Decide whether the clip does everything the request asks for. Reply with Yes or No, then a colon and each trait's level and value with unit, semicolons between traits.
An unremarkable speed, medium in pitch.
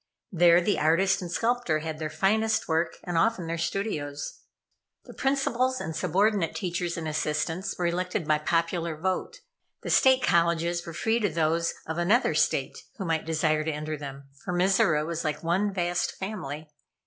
Yes: average, 170 wpm; medium, 170 Hz